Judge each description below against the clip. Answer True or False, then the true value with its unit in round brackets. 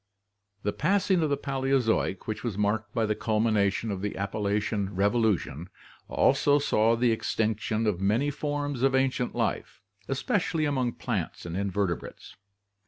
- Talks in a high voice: False (110 Hz)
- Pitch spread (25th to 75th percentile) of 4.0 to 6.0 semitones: True (4.9 semitones)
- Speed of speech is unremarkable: True (150 wpm)